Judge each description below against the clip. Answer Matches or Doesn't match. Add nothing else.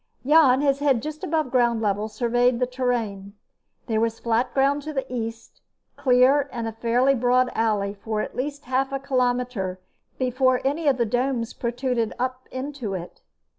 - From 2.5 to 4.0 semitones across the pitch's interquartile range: Matches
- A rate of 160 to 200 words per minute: Matches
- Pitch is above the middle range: Matches